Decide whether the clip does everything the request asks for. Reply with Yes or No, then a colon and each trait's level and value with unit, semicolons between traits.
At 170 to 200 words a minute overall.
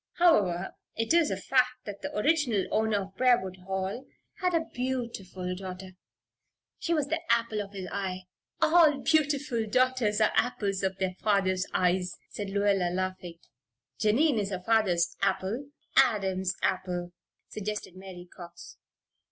No: average, 145 wpm